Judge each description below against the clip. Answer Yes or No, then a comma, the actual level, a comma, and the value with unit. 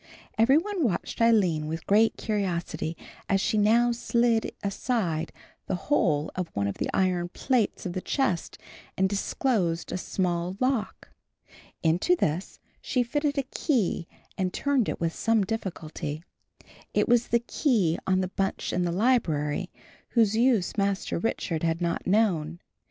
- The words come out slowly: No, average, 150 wpm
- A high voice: Yes, high, 195 Hz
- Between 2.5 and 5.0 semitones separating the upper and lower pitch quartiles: No, wide, 5.5 semitones